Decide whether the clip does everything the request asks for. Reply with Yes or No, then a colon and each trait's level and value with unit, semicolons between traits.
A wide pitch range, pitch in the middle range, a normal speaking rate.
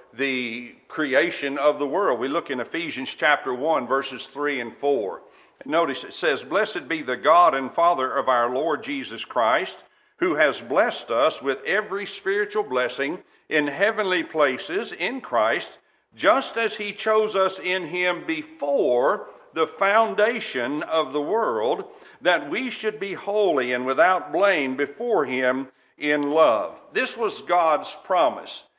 Yes: wide, 7.7 semitones; medium, 180 Hz; average, 150 wpm